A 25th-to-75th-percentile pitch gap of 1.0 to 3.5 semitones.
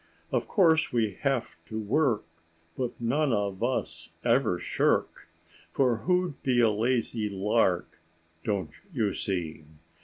No: average, 4.4 semitones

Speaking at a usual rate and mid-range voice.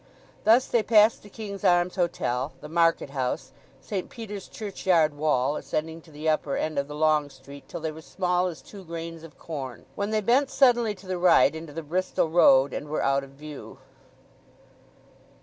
Yes: average, 185 wpm; medium, 165 Hz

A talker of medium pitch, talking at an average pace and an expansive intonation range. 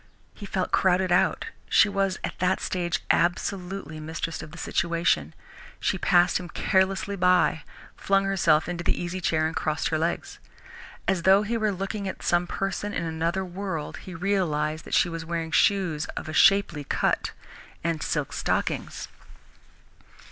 No: medium, 175 Hz; average, 155 wpm; average, 3.0 semitones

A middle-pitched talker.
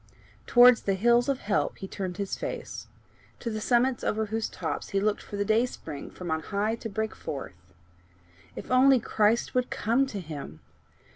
No: high, 215 Hz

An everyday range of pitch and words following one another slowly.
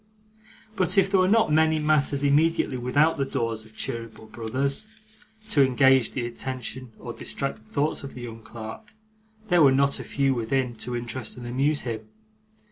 No: average, 4.2 semitones; average, 175 wpm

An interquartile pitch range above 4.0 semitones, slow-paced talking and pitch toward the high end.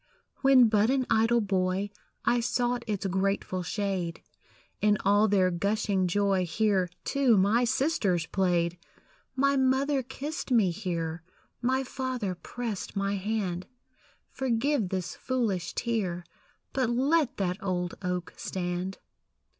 Yes: average, 4.9 semitones; slow, 120 wpm; high, 205 Hz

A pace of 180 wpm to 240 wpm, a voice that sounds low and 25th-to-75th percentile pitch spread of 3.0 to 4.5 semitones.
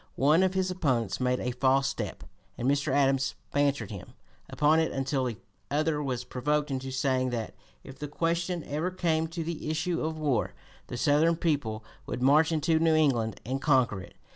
No: average, 185 wpm; medium, 145 Hz; average, 3.7 semitones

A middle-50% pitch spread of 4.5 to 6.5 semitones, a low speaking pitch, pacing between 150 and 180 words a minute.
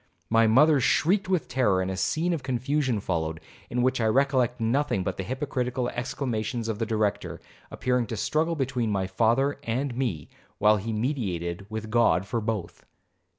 No: average, 4.1 semitones; low, 120 Hz; average, 170 wpm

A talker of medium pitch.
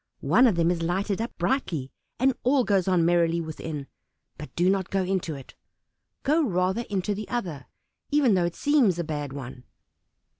Yes: medium, 180 Hz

